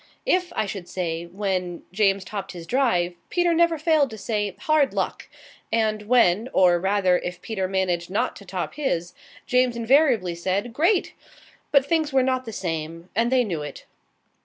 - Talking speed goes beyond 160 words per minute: Yes, average, 170 wpm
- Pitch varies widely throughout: Yes, wide, 6.4 semitones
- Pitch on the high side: Yes, high, 205 Hz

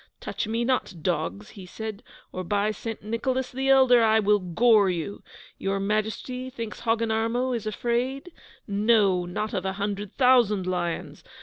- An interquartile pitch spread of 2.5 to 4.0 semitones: Yes, average, 3.4 semitones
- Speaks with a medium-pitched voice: No, high, 215 Hz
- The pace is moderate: Yes, average, 150 wpm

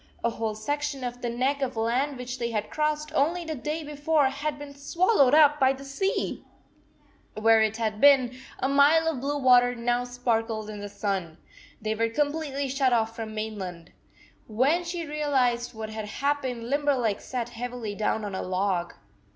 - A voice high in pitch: Yes, very high, 250 Hz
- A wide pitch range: No, average, 4.6 semitones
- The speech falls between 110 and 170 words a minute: No, average, 185 wpm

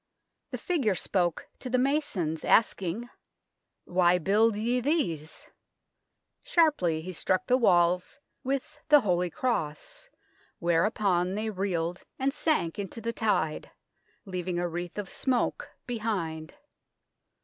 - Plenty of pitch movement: Yes, wide, 5.9 semitones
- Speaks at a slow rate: Yes, slow, 125 wpm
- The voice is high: Yes, high, 195 Hz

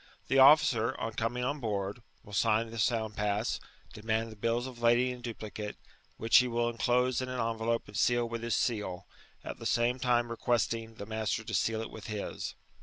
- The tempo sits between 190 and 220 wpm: Yes, average, 195 wpm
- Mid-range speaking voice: No, low, 115 Hz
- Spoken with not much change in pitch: Yes, narrow, 1.7 semitones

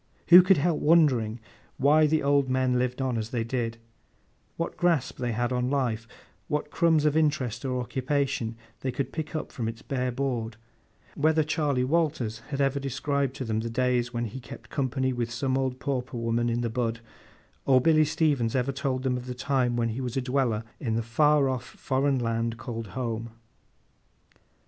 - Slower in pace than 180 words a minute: No, average, 185 wpm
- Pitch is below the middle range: Yes, low, 130 Hz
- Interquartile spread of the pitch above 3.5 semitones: No, average, 3.0 semitones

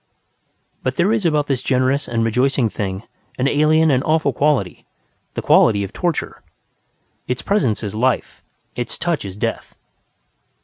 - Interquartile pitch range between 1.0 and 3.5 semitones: No, average, 5.1 semitones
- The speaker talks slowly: No, average, 145 wpm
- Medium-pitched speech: No, low, 130 Hz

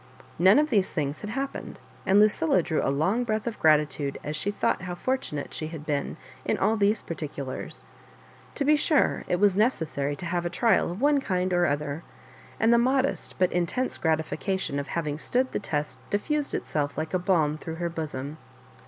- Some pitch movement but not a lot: No, wide, 6.0 semitones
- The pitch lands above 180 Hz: No, medium, 175 Hz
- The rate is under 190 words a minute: No, average, 195 wpm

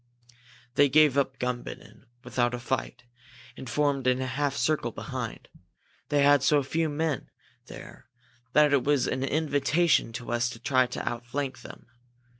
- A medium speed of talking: Yes, average, 155 wpm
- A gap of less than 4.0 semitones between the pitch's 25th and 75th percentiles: Yes, narrow, 2.5 semitones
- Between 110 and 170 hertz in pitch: Yes, low, 135 Hz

